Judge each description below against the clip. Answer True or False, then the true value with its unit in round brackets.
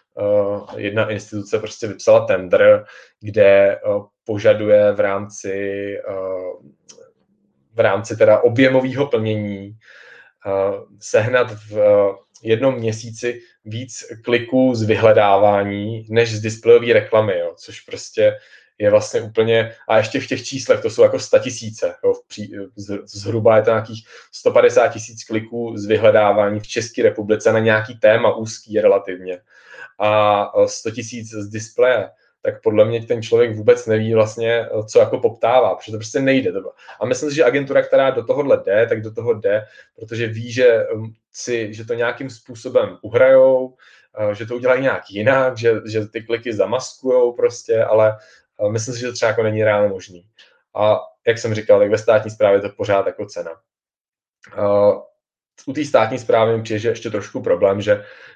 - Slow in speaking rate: False (155 wpm)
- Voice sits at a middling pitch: False (115 Hz)